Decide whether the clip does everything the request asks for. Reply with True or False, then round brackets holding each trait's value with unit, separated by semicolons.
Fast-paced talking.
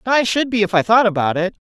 True (290 wpm)